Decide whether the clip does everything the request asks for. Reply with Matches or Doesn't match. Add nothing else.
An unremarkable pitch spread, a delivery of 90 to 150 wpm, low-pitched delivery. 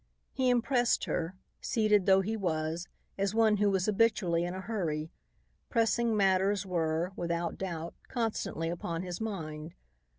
Doesn't match